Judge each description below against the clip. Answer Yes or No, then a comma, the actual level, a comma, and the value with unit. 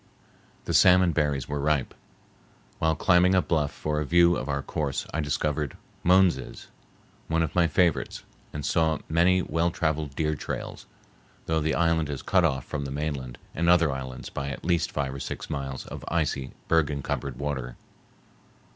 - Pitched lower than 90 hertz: Yes, very low, 75 Hz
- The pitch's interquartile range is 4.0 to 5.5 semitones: No, average, 3.1 semitones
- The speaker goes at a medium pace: Yes, average, 170 wpm